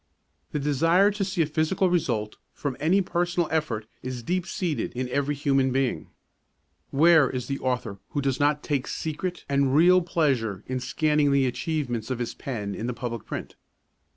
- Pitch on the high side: No, medium, 140 Hz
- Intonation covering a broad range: No, average, 4.5 semitones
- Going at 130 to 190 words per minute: Yes, average, 175 wpm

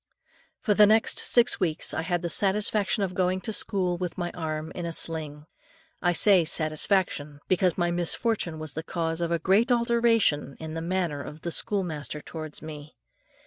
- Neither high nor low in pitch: Yes, medium, 175 Hz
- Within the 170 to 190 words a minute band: Yes, average, 180 wpm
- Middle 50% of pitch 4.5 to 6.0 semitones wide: No, average, 3.6 semitones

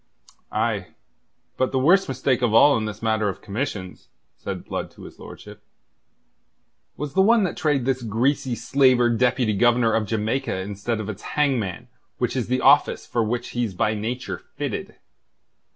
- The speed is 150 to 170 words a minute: Yes, average, 165 wpm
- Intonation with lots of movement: No, average, 3.5 semitones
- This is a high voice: No, low, 120 Hz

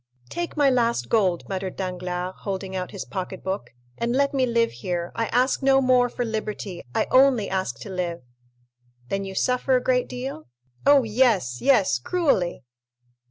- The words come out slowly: No, average, 160 wpm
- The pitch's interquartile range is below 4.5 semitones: No, wide, 5.6 semitones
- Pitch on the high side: Yes, high, 215 Hz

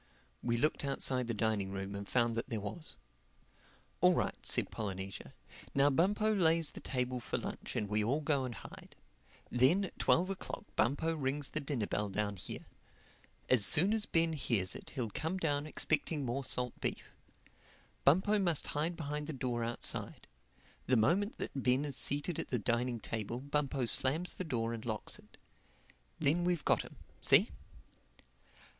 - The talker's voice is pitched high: No, low, 135 Hz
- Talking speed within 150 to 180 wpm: Yes, average, 170 wpm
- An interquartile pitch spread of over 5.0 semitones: Yes, wide, 5.5 semitones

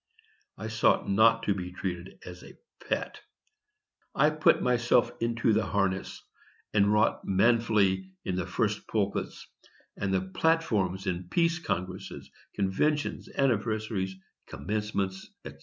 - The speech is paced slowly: Yes, slow, 125 wpm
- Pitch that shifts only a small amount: No, average, 3.3 semitones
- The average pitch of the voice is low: Yes, low, 100 Hz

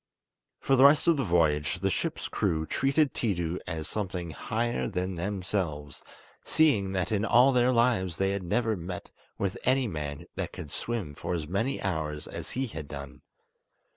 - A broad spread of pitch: Yes, wide, 6.5 semitones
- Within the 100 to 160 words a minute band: No, average, 170 wpm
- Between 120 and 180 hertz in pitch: No, very low, 95 Hz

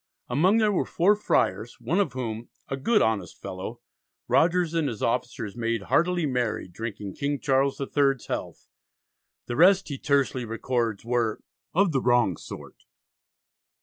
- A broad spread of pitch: Yes, wide, 6.2 semitones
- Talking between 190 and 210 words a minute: No, average, 150 wpm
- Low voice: Yes, low, 130 Hz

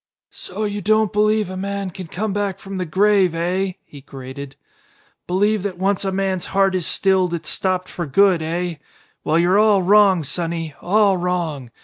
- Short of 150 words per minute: No, average, 175 wpm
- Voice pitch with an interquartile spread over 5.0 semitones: No, narrow, 2.6 semitones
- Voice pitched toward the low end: No, medium, 185 Hz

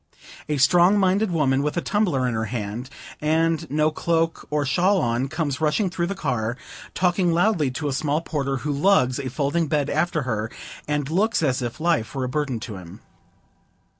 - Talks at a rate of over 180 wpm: Yes, average, 190 wpm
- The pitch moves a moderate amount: Yes, average, 4.7 semitones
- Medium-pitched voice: Yes, medium, 150 Hz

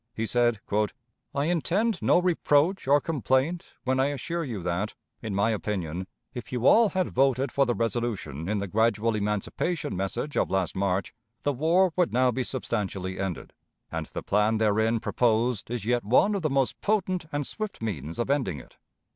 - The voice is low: Yes, low, 120 Hz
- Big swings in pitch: Yes, wide, 5.9 semitones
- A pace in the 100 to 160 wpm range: No, average, 180 wpm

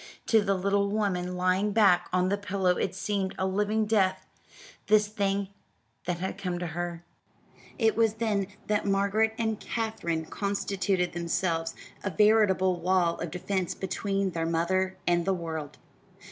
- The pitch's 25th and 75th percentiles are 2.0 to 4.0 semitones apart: Yes, narrow, 2.5 semitones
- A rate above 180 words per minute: No, average, 150 wpm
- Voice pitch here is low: No, high, 190 Hz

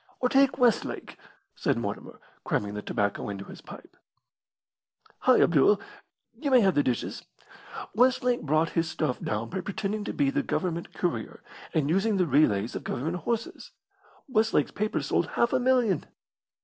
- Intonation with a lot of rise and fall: Yes, wide, 8.4 semitones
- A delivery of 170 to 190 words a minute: No, average, 155 wpm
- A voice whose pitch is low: No, high, 190 Hz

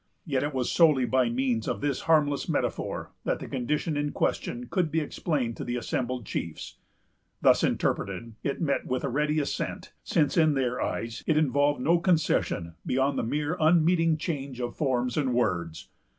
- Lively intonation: No, average, 3.8 semitones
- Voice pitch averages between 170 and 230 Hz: No, medium, 140 Hz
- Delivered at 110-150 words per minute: No, average, 175 wpm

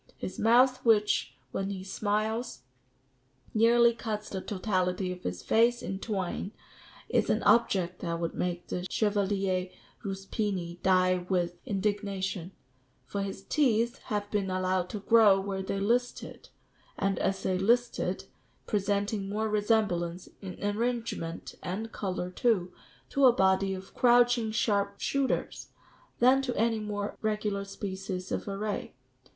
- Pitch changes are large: No, average, 2.9 semitones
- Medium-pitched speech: No, high, 200 Hz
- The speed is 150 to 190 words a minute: No, slow, 135 wpm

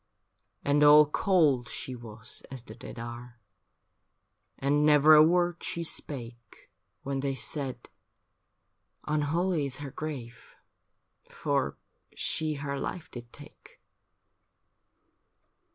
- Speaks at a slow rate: Yes, slow, 110 wpm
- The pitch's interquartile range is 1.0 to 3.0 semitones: No, average, 3.7 semitones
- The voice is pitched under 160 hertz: Yes, medium, 140 Hz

